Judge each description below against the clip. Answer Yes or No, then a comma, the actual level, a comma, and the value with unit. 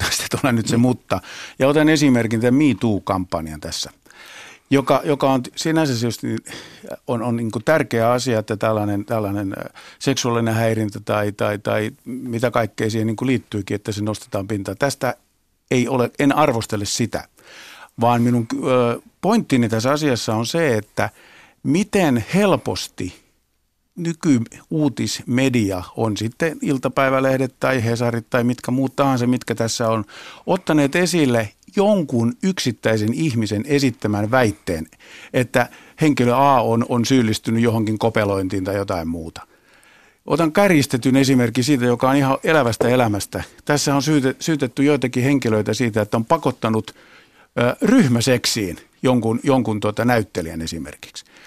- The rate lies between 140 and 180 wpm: No, average, 125 wpm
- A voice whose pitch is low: Yes, low, 120 Hz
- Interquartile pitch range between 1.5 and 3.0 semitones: No, average, 3.8 semitones